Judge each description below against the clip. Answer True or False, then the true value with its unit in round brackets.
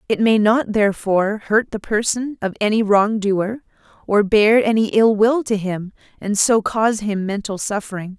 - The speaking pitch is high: True (210 Hz)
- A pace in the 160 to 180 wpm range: True (175 wpm)